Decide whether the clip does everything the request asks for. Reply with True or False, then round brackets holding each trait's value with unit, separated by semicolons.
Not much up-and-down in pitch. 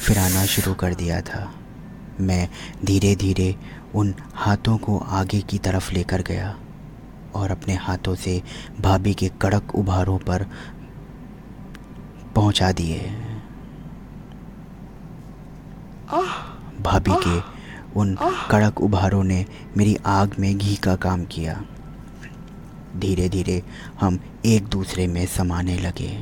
True (1.9 semitones)